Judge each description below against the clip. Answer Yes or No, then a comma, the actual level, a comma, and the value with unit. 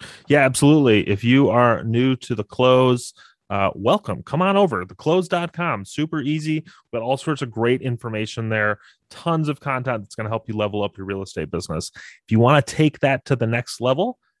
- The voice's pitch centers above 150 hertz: No, low, 130 Hz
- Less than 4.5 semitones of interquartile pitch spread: No, average, 5.3 semitones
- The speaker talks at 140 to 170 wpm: No, fast, 205 wpm